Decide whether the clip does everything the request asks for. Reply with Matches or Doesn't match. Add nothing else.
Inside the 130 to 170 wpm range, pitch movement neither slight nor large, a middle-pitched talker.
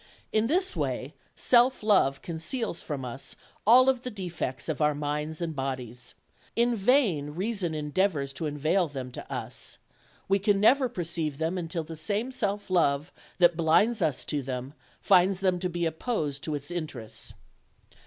Doesn't match